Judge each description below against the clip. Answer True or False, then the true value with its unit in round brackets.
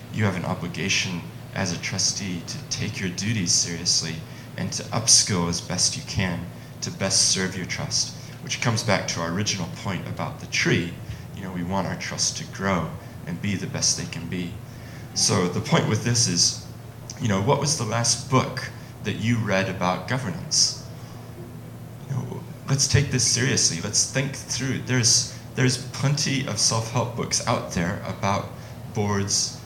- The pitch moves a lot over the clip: False (4.6 semitones)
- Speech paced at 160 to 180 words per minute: True (175 wpm)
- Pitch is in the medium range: False (120 Hz)